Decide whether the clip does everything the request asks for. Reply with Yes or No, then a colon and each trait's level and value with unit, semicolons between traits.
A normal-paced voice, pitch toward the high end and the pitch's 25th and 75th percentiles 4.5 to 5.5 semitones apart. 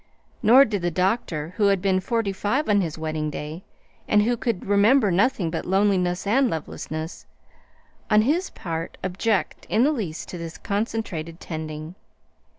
Yes: average, 155 wpm; high, 195 Hz; average, 5.0 semitones